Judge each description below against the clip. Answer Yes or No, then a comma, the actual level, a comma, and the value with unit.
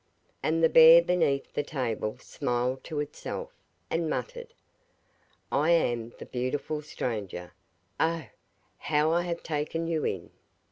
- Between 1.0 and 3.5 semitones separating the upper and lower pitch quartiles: No, average, 4.6 semitones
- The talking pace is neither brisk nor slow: No, slow, 130 wpm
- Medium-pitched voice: Yes, medium, 150 Hz